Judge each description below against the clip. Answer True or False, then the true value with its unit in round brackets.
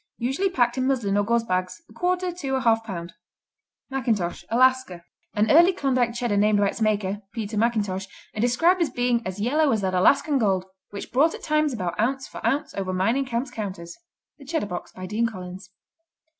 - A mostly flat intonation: False (5.1 semitones)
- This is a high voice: True (230 Hz)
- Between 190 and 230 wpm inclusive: True (195 wpm)